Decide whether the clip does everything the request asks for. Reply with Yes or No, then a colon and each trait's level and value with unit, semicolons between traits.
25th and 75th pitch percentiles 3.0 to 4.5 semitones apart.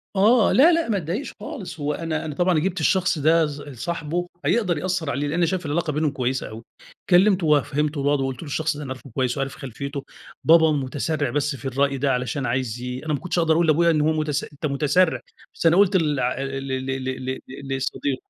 Yes: average, 3.7 semitones